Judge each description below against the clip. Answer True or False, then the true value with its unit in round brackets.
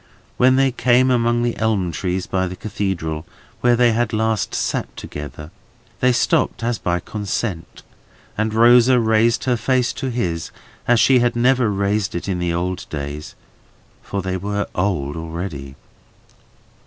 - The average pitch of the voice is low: True (105 Hz)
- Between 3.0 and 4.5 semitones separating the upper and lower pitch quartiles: False (5.3 semitones)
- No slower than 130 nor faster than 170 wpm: True (150 wpm)